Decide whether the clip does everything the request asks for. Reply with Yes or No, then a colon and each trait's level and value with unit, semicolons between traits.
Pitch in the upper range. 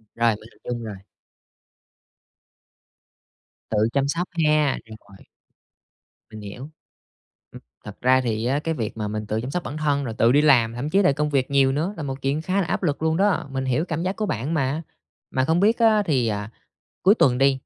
No: low, 135 Hz